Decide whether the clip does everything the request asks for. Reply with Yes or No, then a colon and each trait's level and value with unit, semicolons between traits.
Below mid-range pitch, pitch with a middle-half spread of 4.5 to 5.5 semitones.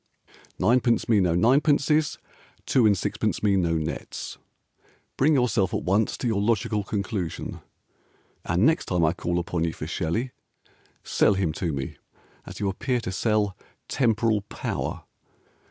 Yes: low, 105 Hz; average, 4.9 semitones